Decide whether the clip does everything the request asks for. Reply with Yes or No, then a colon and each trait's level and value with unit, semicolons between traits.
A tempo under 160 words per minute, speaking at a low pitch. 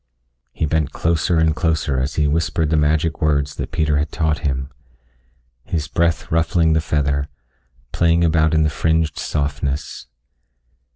Yes: average, 150 wpm; very low, 80 Hz